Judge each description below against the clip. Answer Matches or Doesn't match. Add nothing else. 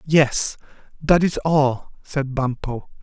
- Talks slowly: Matches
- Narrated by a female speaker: Doesn't match